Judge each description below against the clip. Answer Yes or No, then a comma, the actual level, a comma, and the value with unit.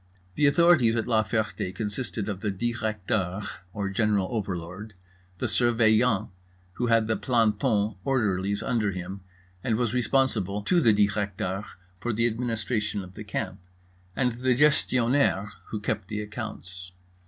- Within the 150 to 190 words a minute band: No, average, 140 wpm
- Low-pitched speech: Yes, low, 110 Hz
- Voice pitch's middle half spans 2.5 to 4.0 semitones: Yes, average, 3.1 semitones